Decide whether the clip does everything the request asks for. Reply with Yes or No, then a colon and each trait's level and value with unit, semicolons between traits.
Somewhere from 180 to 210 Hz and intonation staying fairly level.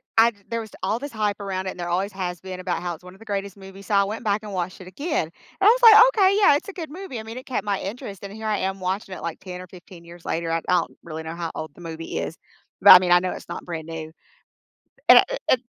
No: high, 190 Hz; average, 3.9 semitones